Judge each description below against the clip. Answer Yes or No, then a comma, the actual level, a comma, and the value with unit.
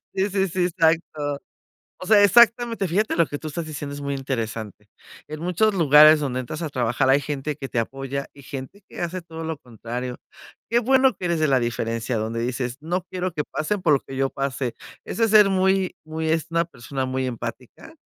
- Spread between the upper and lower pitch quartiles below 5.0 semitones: No, wide, 5.5 semitones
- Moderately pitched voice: Yes, medium, 150 Hz